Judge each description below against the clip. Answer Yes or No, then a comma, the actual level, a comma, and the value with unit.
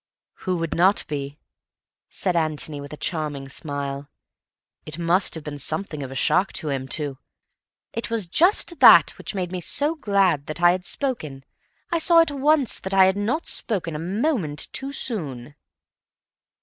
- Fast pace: No, average, 170 wpm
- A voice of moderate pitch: Yes, medium, 175 Hz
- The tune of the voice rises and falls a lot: Yes, wide, 6.6 semitones